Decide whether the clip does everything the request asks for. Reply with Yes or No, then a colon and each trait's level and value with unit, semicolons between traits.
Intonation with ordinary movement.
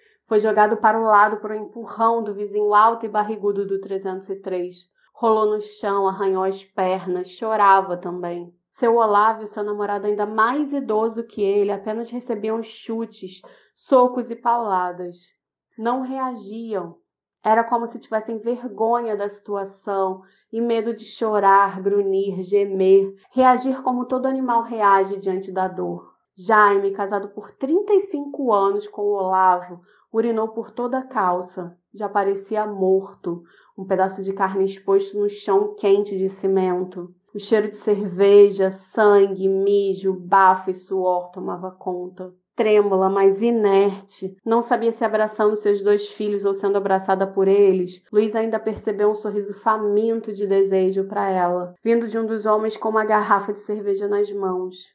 No: narrow, 2.3 semitones